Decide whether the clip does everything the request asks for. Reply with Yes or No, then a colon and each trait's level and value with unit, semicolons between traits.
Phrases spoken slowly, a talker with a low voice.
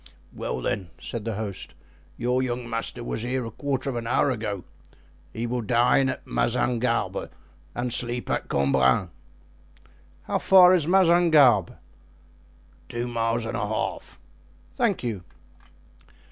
Yes: slow, 130 wpm; low, 120 Hz